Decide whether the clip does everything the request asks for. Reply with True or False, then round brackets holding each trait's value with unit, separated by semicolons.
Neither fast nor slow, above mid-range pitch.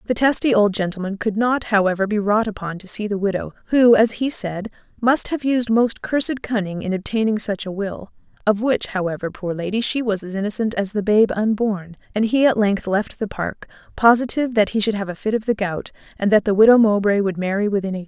False (230 wpm; 210 Hz)